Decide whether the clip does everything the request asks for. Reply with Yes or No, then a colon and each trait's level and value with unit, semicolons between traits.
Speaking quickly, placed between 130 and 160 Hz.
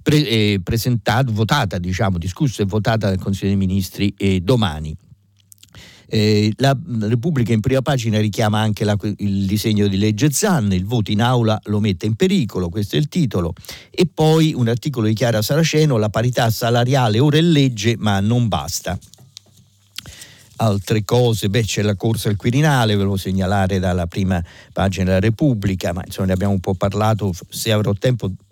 No: fast, 175 wpm; low, 110 Hz